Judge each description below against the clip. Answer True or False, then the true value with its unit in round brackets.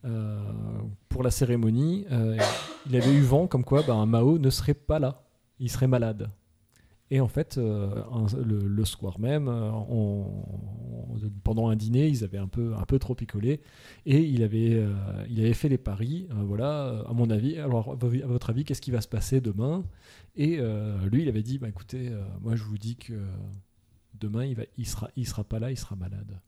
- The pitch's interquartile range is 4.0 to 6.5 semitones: False (3.5 semitones)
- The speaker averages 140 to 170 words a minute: False (215 wpm)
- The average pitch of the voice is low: True (115 Hz)